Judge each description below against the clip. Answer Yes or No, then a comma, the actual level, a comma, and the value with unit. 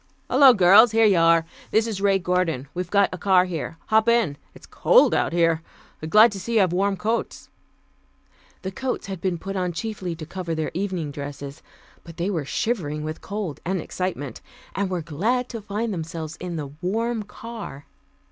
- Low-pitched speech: No, medium, 185 Hz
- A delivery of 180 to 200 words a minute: Yes, average, 185 wpm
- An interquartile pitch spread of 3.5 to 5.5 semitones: Yes, average, 4.3 semitones